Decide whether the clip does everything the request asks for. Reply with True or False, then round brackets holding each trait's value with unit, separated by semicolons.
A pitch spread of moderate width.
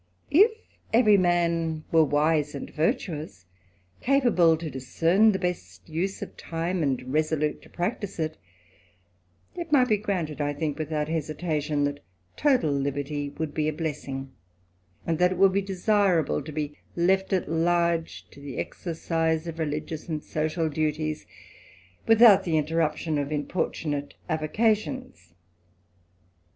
True (3.5 semitones)